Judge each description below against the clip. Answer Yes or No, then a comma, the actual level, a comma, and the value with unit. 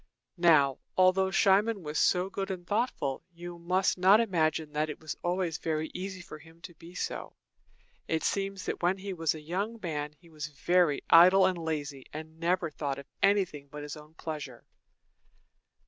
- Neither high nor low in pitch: Yes, medium, 170 Hz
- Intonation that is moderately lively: Yes, average, 3.6 semitones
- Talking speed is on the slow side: No, average, 180 wpm